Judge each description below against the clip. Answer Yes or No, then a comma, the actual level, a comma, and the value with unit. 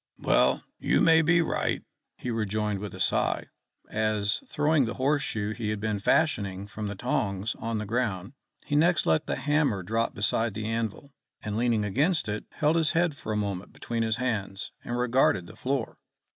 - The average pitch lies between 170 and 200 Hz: No, low, 115 Hz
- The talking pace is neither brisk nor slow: Yes, average, 185 wpm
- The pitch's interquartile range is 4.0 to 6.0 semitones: Yes, average, 5.0 semitones